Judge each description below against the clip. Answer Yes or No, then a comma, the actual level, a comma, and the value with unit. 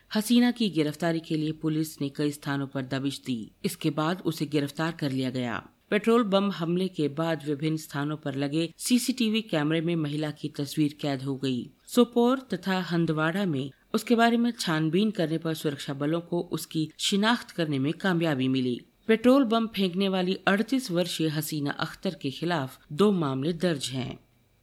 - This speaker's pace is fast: No, average, 170 wpm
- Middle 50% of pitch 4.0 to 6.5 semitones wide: Yes, average, 4.9 semitones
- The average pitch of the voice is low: No, medium, 160 Hz